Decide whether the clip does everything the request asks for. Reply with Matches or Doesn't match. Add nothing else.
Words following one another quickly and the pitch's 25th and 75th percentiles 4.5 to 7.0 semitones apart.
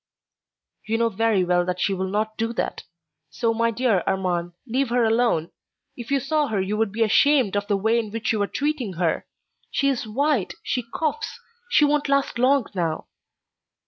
Doesn't match